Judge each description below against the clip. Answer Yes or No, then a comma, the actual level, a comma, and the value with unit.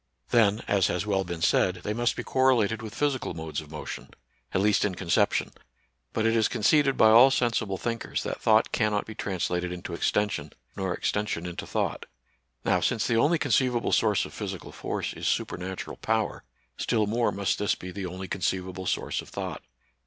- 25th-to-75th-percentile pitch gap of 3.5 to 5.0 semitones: Yes, average, 4.0 semitones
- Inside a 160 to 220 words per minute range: Yes, average, 180 wpm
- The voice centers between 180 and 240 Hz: No, low, 105 Hz